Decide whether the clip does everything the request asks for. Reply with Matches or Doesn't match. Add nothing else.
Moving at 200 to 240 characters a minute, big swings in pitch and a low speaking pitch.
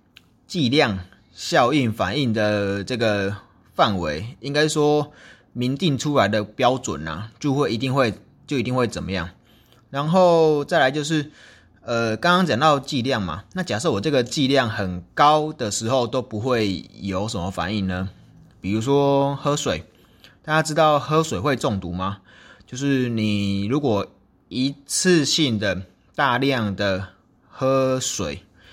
Matches